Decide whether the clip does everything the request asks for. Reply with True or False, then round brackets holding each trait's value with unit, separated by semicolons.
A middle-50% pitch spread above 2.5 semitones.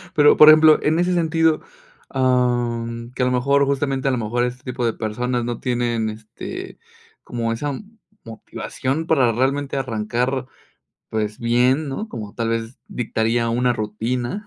True (2.9 semitones)